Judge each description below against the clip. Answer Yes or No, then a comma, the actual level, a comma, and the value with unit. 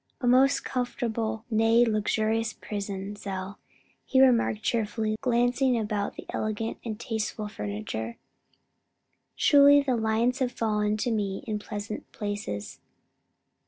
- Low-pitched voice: No, high, 220 Hz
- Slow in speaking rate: Yes, slow, 125 wpm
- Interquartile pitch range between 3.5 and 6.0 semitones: No, narrow, 2.6 semitones